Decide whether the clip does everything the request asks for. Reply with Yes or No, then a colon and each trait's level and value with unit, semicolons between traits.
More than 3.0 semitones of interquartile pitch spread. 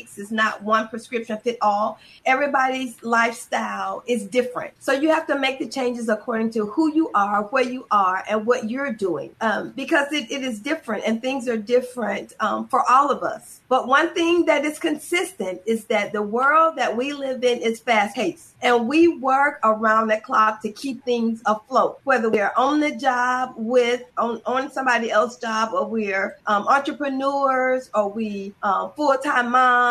Yes: average, 3.7 semitones